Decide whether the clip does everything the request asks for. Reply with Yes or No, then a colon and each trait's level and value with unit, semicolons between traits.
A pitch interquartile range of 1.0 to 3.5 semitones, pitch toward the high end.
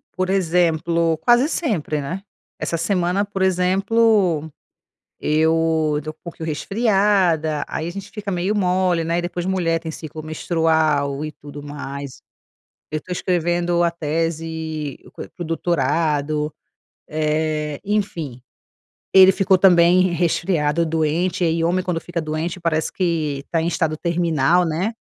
No: average, 2.7 semitones; medium, 165 Hz